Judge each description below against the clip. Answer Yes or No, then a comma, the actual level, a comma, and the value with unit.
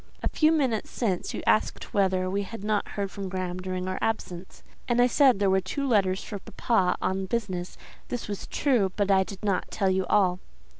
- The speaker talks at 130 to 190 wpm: No, fast, 205 wpm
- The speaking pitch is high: Yes, high, 195 Hz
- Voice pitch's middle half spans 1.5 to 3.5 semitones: Yes, average, 3.0 semitones